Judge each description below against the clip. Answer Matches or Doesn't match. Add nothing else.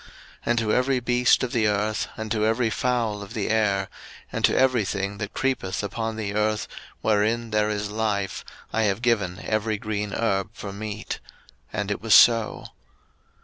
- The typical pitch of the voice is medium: Doesn't match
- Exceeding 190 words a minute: Doesn't match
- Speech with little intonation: Matches